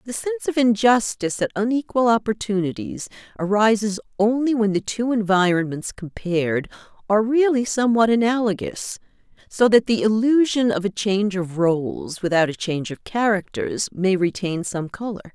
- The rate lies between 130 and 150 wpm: Yes, average, 140 wpm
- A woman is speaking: Yes, female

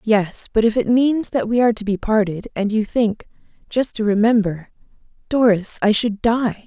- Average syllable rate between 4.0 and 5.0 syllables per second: Yes, 4.8 syllables/s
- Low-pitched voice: No, high, 220 Hz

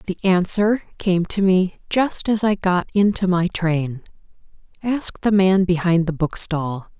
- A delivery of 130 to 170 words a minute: Yes, average, 155 wpm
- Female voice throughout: Yes, female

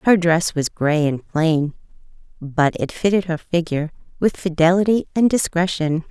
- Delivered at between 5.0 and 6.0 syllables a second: No, 4.7 syllables/s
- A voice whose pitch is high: No, medium, 170 Hz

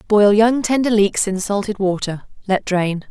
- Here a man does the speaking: No, female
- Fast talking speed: No, average, 175 wpm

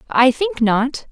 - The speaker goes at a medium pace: Yes, average, 160 wpm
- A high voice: Yes, very high, 265 Hz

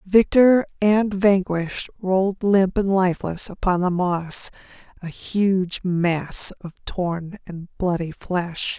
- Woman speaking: Yes, female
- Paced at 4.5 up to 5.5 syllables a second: No, 3.5 syllables/s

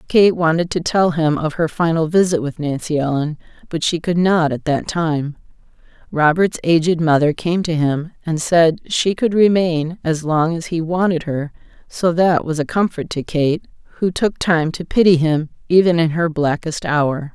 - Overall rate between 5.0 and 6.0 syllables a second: No, 4.5 syllables/s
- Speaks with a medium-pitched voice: Yes, medium, 165 Hz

